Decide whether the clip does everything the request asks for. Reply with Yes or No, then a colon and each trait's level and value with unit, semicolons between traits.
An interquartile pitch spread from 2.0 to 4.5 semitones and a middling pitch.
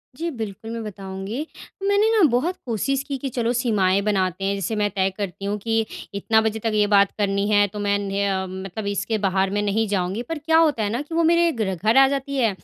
No: average, 3.9 semitones; high, 210 Hz